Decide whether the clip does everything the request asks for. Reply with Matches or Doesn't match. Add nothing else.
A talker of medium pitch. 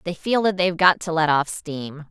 Matches